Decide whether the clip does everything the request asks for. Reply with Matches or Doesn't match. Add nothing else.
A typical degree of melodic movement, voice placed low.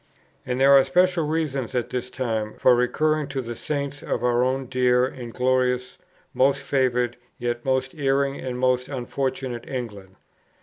Doesn't match